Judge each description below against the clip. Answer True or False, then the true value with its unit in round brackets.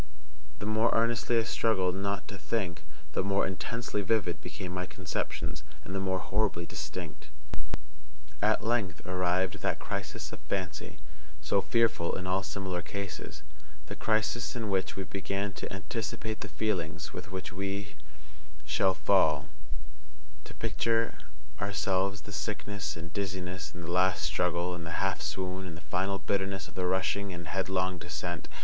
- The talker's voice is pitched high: False (95 Hz)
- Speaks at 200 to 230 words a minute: False (150 wpm)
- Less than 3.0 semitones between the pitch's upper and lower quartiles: True (2.6 semitones)